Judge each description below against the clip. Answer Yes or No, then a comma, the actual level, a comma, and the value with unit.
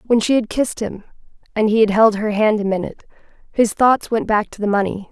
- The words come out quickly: Yes, fast, 235 wpm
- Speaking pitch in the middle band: No, high, 215 Hz